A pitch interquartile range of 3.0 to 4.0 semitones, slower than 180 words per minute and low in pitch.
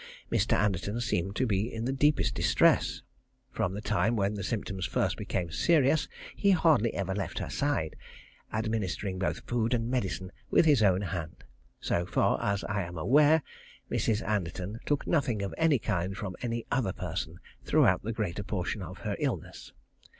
No: average, 4.5 semitones; average, 170 wpm; low, 105 Hz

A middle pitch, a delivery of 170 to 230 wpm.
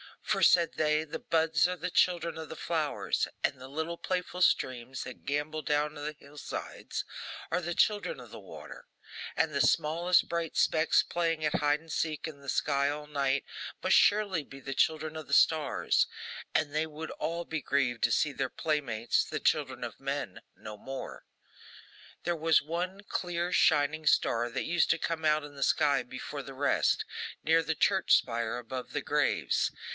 Yes: medium, 155 Hz; average, 180 wpm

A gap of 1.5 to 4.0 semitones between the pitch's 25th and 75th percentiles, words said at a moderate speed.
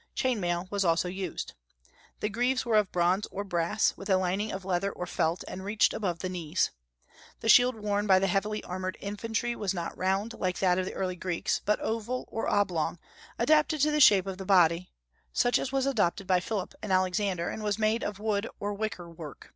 No: average, 3.0 semitones; fast, 210 wpm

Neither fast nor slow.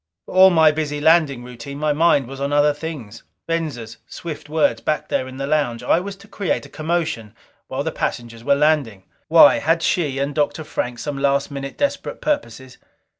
Yes: average, 190 wpm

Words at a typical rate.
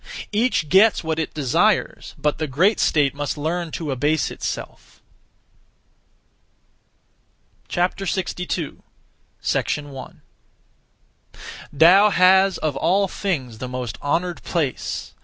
No: slow, 100 wpm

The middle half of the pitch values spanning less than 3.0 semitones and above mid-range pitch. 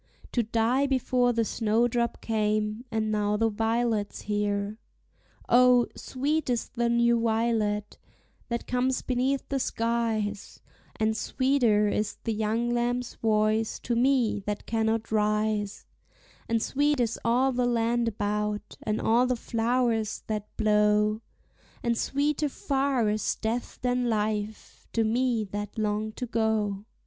Yes: narrow, 2.4 semitones; high, 225 Hz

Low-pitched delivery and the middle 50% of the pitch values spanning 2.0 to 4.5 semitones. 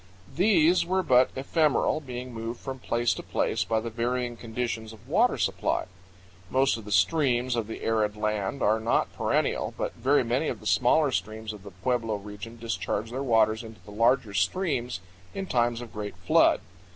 Yes: low, 120 Hz; average, 3.3 semitones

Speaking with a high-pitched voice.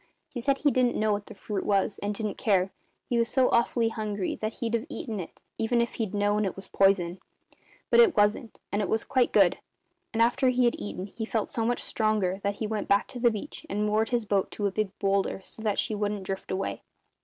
Yes: high, 215 Hz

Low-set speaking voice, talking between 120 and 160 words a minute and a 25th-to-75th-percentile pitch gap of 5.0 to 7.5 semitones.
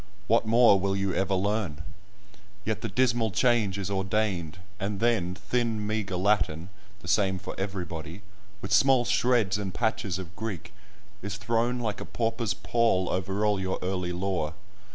No: low, 100 Hz; average, 155 wpm; average, 3.2 semitones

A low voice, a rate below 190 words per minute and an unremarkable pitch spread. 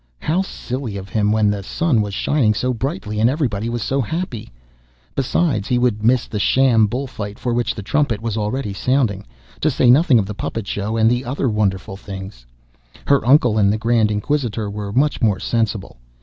No: low, 115 Hz; average, 195 wpm; average, 3.9 semitones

